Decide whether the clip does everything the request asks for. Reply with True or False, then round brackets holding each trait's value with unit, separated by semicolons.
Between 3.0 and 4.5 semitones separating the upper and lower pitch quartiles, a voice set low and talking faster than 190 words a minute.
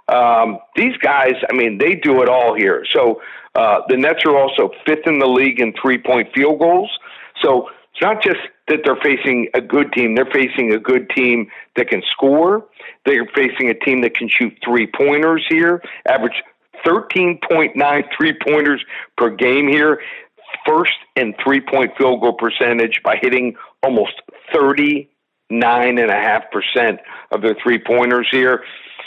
False (3.6 semitones; 130 Hz; 160 wpm)